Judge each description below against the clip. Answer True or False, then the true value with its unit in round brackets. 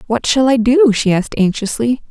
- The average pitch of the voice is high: True (240 Hz)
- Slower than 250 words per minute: True (200 wpm)